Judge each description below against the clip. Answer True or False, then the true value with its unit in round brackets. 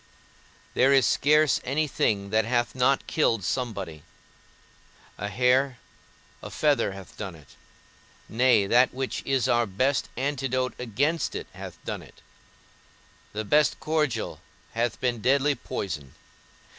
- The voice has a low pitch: True (125 Hz)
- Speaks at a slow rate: True (130 wpm)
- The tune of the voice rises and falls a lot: False (3.9 semitones)